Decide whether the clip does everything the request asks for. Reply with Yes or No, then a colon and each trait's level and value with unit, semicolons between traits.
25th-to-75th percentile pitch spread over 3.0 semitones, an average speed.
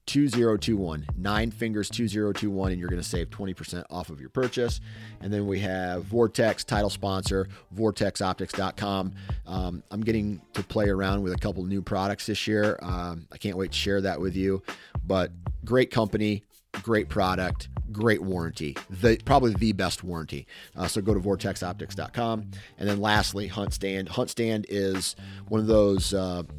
No: narrow, 2.6 semitones; average, 165 wpm